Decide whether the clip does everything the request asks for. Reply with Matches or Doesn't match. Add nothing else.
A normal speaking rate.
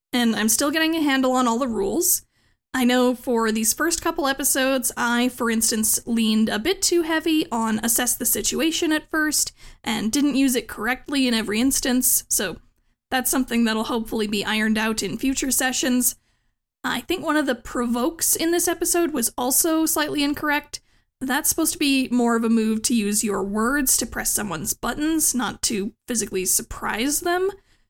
Matches